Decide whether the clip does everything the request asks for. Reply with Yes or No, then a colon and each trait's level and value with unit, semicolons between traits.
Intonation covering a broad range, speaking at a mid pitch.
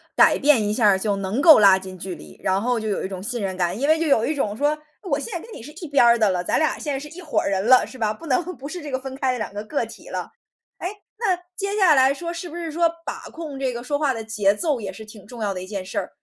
No: wide, 6.6 semitones; high, 245 Hz